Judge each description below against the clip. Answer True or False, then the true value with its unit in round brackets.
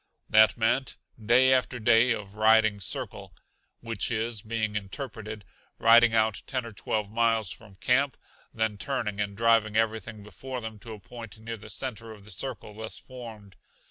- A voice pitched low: True (110 Hz)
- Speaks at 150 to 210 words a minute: True (165 wpm)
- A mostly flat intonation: True (1.9 semitones)